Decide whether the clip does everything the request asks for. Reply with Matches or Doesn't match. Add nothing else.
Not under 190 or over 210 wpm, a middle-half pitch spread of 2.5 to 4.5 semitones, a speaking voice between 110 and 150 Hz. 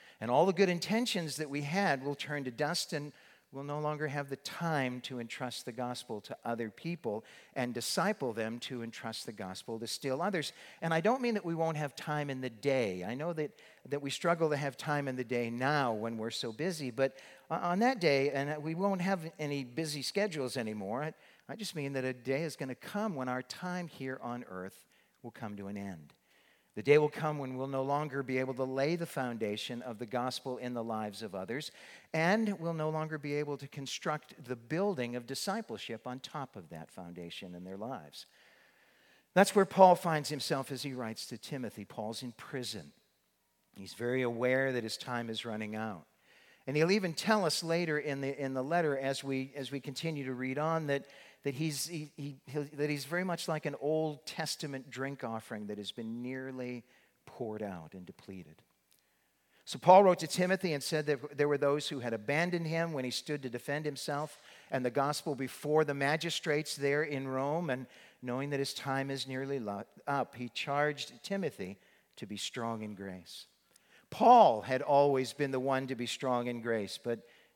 Matches